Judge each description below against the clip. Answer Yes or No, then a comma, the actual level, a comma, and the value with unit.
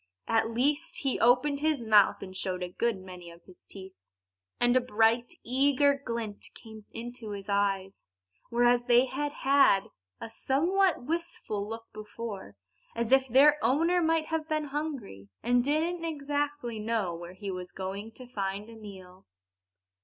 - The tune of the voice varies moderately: No, wide, 5.9 semitones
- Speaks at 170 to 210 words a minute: No, average, 155 wpm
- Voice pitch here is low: No, high, 235 Hz